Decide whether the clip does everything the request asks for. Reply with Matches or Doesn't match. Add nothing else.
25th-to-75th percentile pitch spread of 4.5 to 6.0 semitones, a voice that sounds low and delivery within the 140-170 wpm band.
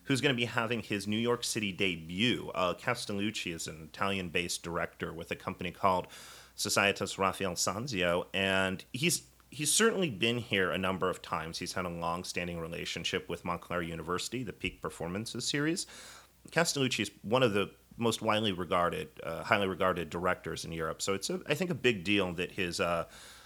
Doesn't match